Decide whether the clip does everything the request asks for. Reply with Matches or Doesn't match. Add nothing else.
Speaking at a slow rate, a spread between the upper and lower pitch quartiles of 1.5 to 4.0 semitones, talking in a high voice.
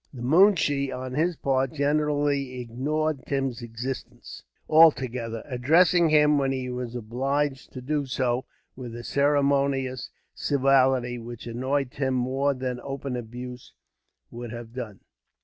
Doesn't match